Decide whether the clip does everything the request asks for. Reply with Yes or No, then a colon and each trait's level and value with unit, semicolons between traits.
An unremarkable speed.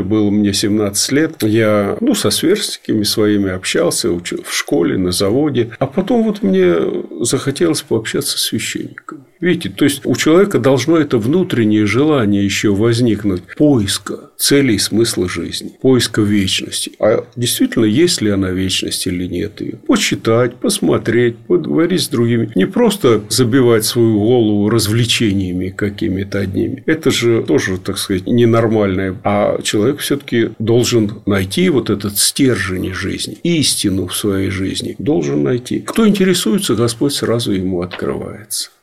Yes: average, 140 wpm